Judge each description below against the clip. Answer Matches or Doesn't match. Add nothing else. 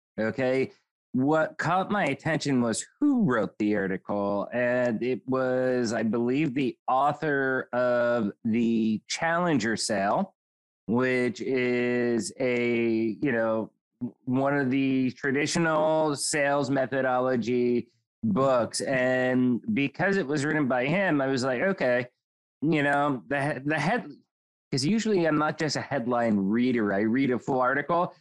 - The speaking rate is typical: Doesn't match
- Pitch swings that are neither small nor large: Matches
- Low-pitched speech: Matches